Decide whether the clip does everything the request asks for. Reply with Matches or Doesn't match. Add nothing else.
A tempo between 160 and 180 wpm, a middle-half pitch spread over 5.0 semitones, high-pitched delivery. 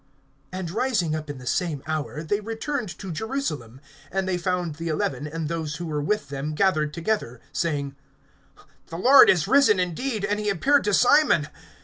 Doesn't match